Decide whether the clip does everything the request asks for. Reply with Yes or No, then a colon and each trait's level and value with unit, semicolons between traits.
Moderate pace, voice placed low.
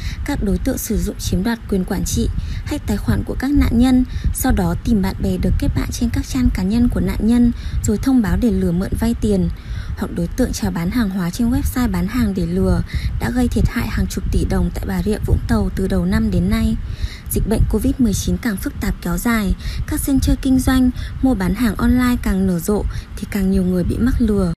No: average, 240 wpm; high, 190 Hz